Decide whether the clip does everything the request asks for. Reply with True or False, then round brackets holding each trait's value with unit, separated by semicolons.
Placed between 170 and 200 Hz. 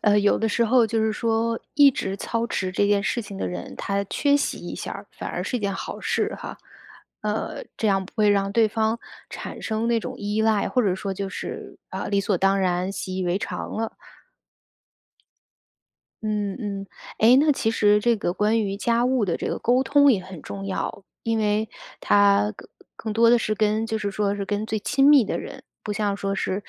False (210 Hz)